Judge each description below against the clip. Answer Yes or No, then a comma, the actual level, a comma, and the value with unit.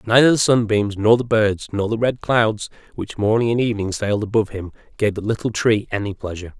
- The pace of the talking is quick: Yes, fast, 210 wpm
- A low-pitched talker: Yes, low, 110 Hz